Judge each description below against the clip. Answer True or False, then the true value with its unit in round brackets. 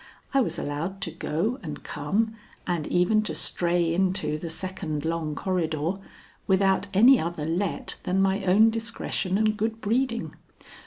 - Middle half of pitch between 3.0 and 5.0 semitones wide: True (4.6 semitones)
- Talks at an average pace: True (150 wpm)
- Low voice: False (185 Hz)